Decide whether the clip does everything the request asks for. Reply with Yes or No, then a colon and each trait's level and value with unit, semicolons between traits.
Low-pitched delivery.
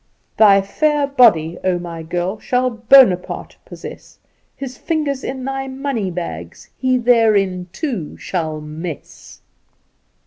No: high, 215 Hz